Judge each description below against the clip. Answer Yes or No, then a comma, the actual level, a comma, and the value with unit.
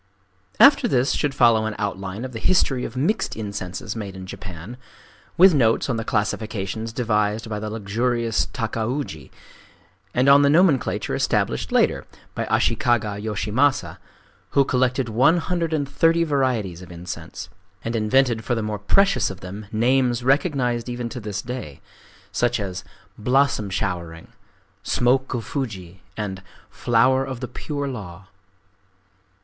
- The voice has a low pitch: Yes, low, 115 Hz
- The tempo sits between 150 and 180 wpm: No, average, 140 wpm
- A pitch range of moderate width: Yes, average, 4.2 semitones